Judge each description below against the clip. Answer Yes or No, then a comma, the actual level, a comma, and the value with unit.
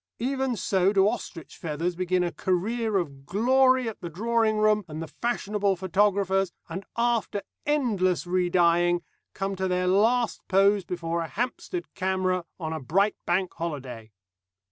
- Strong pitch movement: No, average, 3.6 semitones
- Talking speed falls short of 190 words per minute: Yes, average, 150 wpm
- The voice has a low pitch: No, high, 190 Hz